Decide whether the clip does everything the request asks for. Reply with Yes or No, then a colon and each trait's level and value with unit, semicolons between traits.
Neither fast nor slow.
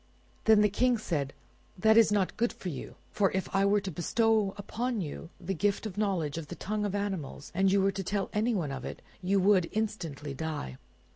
No: fast, 215 wpm